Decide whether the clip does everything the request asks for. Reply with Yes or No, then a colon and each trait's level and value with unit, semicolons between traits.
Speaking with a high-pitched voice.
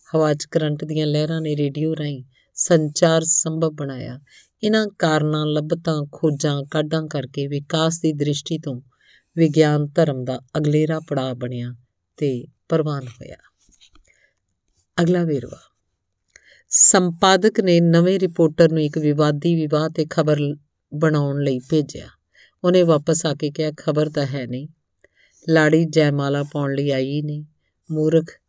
No: medium, 150 Hz